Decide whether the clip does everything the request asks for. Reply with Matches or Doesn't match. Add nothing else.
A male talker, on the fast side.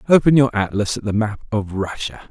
Matches